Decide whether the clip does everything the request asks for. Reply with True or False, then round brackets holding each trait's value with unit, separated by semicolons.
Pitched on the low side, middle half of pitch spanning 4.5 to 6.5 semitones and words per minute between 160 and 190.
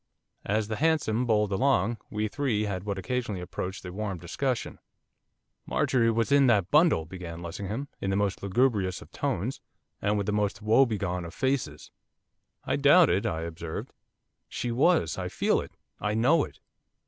True (105 Hz; 5.2 semitones; 165 wpm)